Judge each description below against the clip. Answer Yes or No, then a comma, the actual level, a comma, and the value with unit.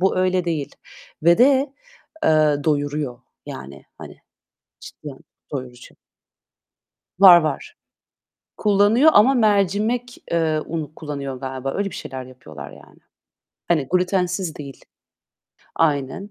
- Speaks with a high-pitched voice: No, medium, 160 Hz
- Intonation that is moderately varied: No, wide, 6.1 semitones